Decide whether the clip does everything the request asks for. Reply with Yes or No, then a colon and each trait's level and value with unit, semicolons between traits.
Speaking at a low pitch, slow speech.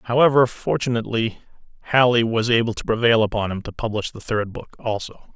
No: low, 115 Hz; average, 170 wpm